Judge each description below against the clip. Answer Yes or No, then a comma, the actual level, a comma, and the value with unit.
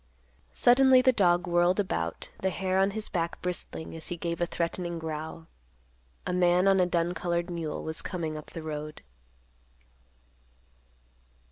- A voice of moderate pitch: Yes, medium, 175 Hz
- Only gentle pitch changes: Yes, narrow, 2.1 semitones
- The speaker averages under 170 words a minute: Yes, average, 150 wpm